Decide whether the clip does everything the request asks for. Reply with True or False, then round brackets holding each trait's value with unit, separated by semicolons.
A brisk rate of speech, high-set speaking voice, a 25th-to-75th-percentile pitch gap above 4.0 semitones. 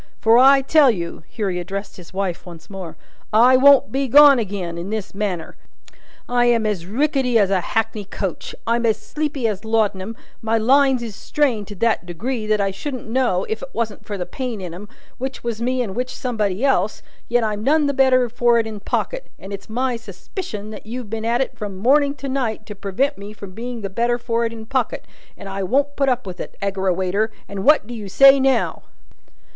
True (215 wpm; 225 Hz; 4.4 semitones)